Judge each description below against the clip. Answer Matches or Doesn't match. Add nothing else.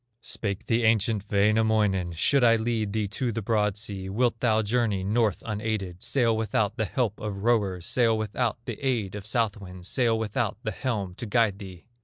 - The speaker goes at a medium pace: Matches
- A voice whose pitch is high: Doesn't match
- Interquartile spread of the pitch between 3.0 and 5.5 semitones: Doesn't match